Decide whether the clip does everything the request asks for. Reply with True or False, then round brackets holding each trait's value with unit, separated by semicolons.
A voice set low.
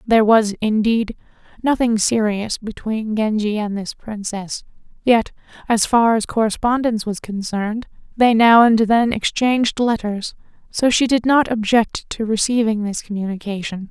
False (220 Hz)